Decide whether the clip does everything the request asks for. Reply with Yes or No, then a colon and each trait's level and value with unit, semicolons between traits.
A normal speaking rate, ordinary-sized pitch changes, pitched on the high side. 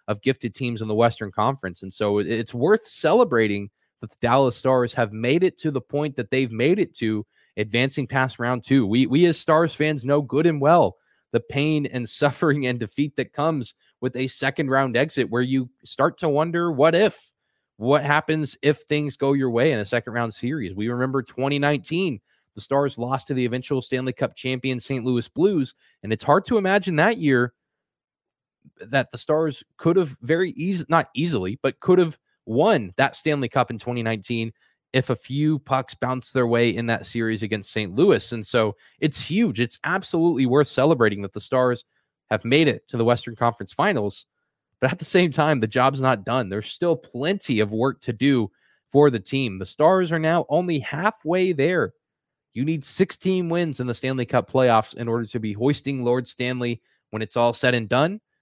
No: average, 195 wpm; average, 4.1 semitones; low, 130 Hz